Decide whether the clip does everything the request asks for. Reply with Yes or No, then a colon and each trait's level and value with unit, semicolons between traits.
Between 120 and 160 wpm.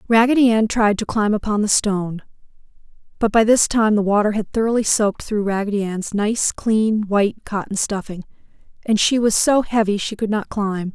No: average, 185 wpm